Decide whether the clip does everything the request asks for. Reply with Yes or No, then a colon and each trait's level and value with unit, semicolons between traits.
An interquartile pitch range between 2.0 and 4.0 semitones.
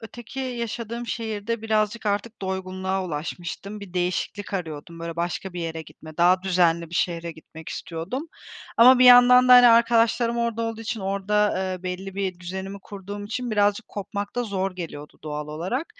No: average, 4.6 semitones